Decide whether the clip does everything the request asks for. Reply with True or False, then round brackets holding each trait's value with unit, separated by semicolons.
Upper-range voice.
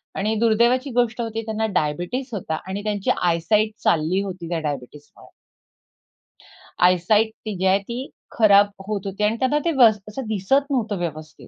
True (205 Hz)